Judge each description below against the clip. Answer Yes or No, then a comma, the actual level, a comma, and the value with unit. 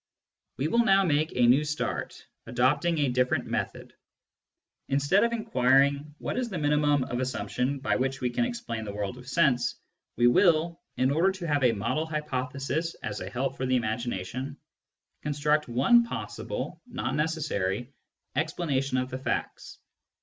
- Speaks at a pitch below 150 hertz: Yes, medium, 140 Hz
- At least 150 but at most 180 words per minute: Yes, average, 155 wpm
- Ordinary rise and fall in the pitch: Yes, average, 3.9 semitones